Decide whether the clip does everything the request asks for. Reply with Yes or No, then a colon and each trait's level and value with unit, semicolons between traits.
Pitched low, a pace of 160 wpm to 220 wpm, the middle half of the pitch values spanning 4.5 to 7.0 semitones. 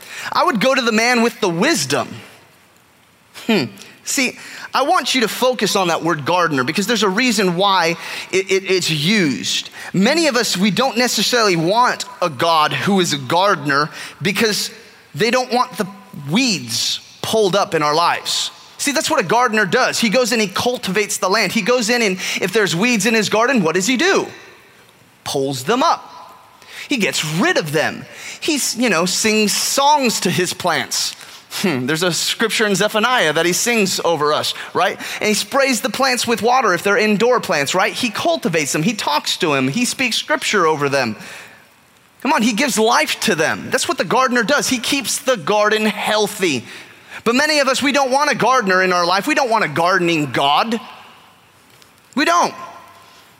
No: high, 215 Hz; average, 190 wpm; average, 5.2 semitones